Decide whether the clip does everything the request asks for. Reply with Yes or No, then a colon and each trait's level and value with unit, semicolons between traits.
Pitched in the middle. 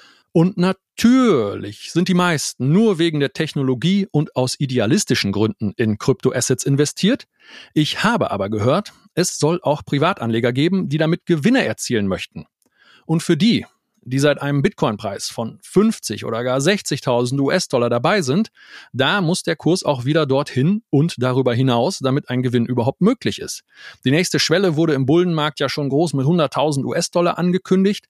Yes: medium, 150 Hz